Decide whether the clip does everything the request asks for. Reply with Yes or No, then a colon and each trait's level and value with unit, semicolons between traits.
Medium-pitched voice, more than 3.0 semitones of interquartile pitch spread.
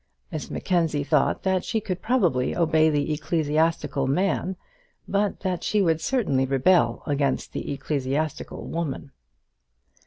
Yes: medium, 160 Hz; average, 4.5 semitones